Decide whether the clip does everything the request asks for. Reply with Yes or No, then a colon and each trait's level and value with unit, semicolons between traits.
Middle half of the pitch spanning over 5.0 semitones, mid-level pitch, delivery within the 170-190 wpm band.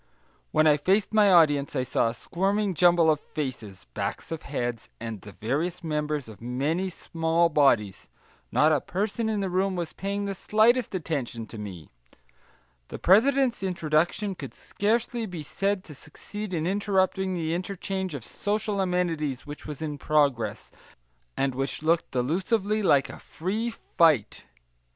No: wide, 5.6 semitones; medium, 170 Hz; average, 155 wpm